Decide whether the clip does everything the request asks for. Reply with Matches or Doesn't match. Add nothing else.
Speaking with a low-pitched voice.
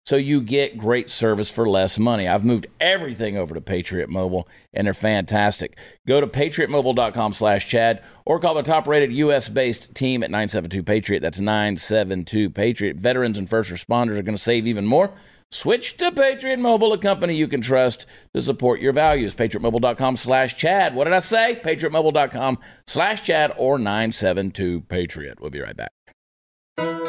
Matches